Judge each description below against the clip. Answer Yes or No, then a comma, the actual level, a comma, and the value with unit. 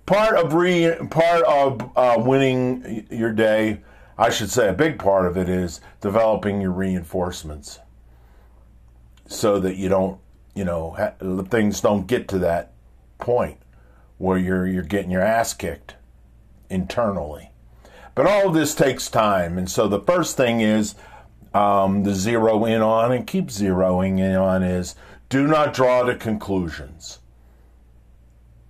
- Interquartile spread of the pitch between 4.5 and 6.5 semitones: Yes, average, 5.0 semitones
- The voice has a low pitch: Yes, very low, 95 Hz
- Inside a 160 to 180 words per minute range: No, average, 145 wpm